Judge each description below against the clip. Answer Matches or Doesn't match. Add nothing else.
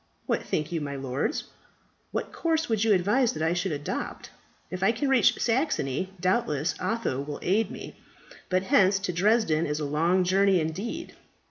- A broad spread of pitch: Matches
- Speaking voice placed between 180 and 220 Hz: Matches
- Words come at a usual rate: Matches